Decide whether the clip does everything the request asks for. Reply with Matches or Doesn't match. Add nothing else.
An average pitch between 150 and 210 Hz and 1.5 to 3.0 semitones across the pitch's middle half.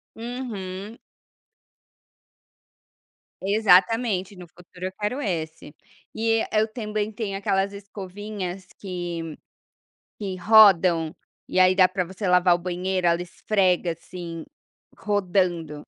Matches